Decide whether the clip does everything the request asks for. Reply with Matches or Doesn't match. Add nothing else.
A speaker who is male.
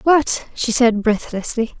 Doesn't match